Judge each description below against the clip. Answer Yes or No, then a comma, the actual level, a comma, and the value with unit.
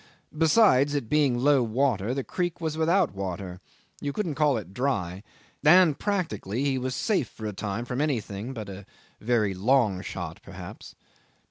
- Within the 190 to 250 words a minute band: No, average, 160 wpm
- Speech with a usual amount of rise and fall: No, wide, 6.7 semitones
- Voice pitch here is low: Yes, low, 125 Hz